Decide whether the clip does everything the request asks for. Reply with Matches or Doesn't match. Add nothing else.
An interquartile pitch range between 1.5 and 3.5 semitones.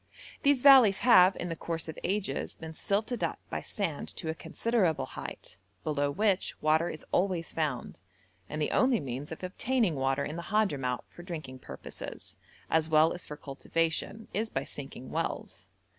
Doesn't match